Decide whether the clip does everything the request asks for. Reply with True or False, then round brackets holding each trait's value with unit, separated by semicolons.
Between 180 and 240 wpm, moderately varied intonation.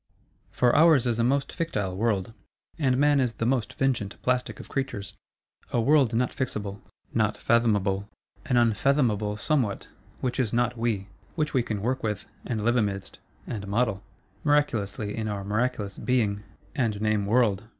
False (155 wpm; 3.8 semitones)